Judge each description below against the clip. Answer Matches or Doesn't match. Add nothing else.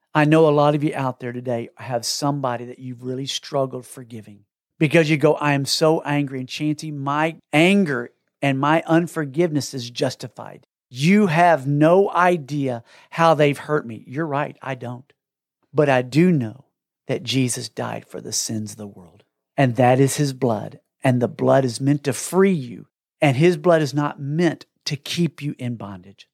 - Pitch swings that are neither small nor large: Matches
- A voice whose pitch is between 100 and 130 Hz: Doesn't match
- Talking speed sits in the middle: Matches